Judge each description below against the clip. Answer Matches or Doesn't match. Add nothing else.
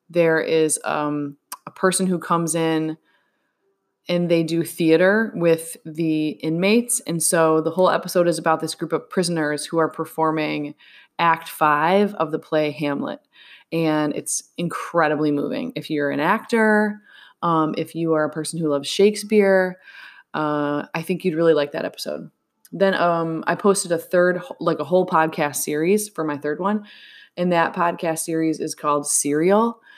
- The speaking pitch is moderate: Matches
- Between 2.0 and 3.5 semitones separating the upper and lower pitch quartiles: Matches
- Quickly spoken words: Doesn't match